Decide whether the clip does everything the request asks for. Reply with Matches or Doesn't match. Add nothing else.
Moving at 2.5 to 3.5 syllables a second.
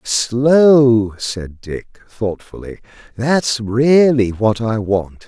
Matches